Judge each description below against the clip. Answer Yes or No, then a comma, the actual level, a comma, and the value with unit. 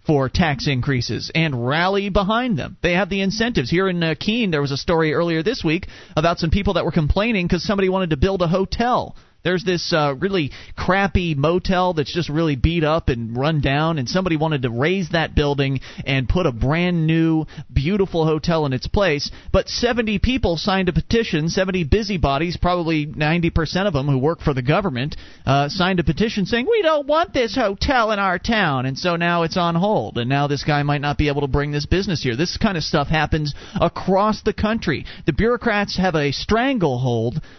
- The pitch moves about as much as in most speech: Yes, average, 4.6 semitones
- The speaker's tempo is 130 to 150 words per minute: No, fast, 205 wpm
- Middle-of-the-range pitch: Yes, medium, 170 Hz